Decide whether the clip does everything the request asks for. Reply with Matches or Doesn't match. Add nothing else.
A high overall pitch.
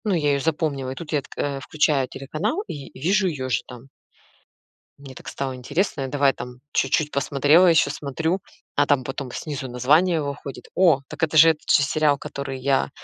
Doesn't match